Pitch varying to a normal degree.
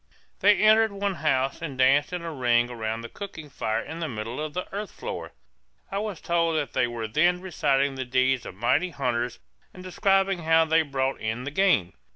No: wide, 6.5 semitones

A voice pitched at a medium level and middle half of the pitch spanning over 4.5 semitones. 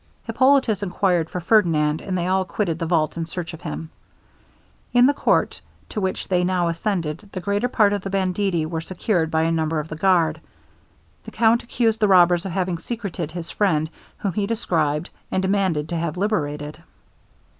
No: medium, 180 Hz; average, 3.7 semitones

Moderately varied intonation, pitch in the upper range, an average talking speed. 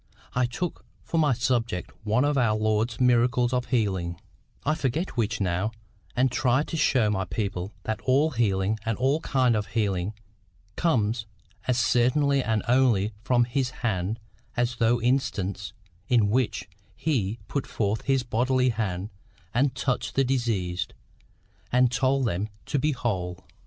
No: average, 3.6 semitones; low, 120 Hz; average, 150 wpm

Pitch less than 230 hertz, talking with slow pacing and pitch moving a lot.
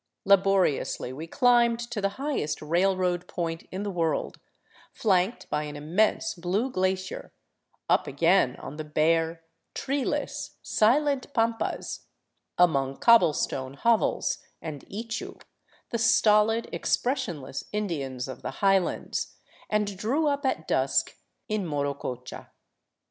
Yes: high, 190 Hz; slow, 115 wpm; wide, 6.3 semitones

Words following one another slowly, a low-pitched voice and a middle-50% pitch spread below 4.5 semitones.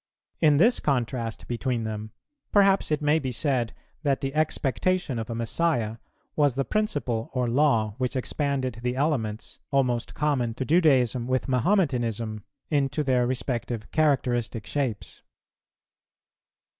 Yes: slow, 130 wpm; low, 130 Hz; average, 4.0 semitones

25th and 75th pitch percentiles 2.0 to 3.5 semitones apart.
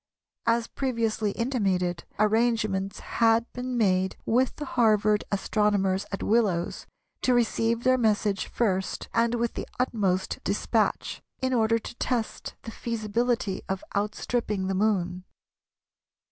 Yes: average, 3.1 semitones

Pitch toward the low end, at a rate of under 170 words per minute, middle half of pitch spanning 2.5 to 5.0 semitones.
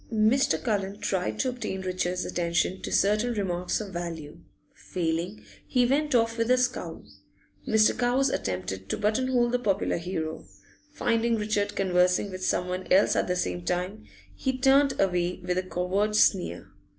No: high, 195 Hz; average, 160 wpm; average, 4.7 semitones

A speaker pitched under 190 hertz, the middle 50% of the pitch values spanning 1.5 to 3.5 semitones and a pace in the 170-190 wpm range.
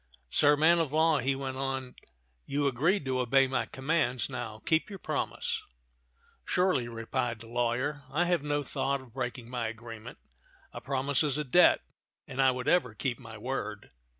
Yes: low, 135 Hz; average, 3.1 semitones; average, 175 wpm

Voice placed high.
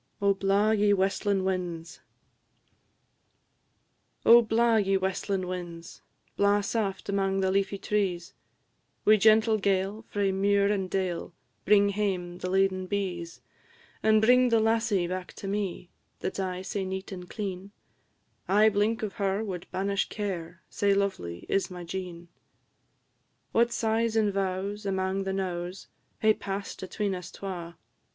Yes: high, 195 Hz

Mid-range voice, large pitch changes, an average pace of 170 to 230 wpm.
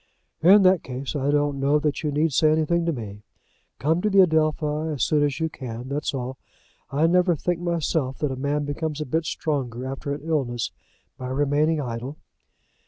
No: medium, 150 Hz; average, 3.1 semitones; average, 190 wpm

